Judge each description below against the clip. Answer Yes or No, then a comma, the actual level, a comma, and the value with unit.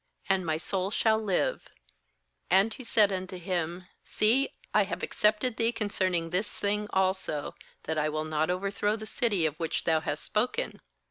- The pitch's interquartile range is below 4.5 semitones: Yes, average, 4.1 semitones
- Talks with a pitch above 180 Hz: Yes, high, 190 Hz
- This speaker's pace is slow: No, average, 180 wpm